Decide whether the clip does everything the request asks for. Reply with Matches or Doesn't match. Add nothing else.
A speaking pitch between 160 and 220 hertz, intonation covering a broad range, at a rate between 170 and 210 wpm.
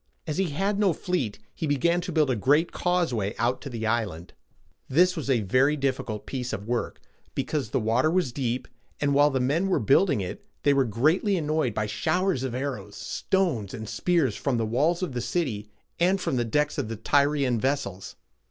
Doesn't match